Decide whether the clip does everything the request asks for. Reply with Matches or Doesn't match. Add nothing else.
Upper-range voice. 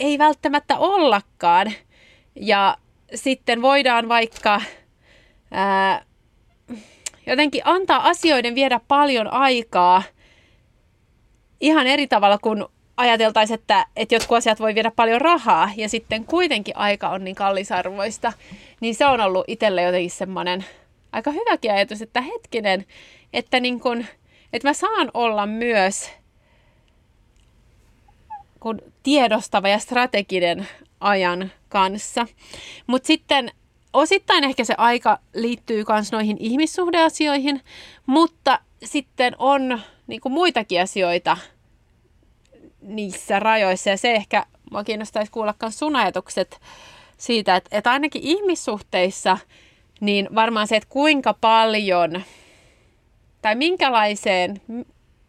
Matches